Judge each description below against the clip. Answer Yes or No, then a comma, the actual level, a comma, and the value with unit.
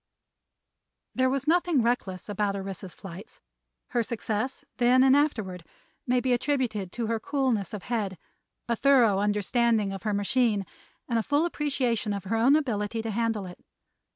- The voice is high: Yes, high, 230 Hz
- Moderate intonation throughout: Yes, average, 4.0 semitones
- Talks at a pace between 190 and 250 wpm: No, average, 155 wpm